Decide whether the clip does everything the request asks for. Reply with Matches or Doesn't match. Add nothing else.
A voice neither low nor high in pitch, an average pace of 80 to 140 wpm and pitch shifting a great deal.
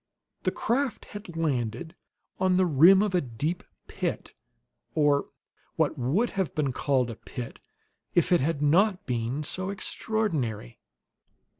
Matches